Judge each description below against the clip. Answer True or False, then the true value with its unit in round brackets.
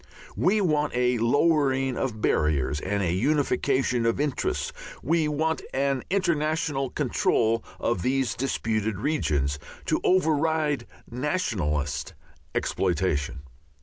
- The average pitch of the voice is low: True (130 Hz)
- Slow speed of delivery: True (105 wpm)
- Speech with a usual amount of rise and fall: False (5.7 semitones)